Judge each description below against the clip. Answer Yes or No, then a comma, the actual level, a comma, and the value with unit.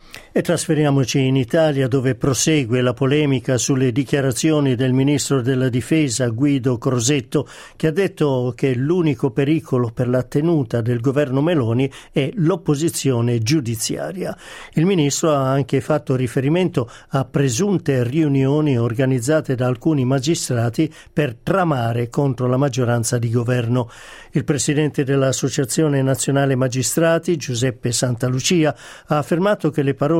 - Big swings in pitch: No, average, 3.1 semitones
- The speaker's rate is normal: Yes, average, 125 wpm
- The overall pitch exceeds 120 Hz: Yes, medium, 140 Hz